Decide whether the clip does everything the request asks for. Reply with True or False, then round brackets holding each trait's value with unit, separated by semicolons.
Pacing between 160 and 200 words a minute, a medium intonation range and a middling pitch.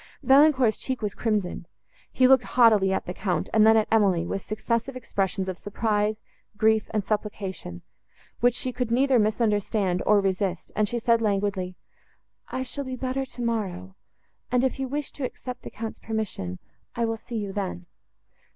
False (165 wpm; 3.9 semitones; 220 Hz)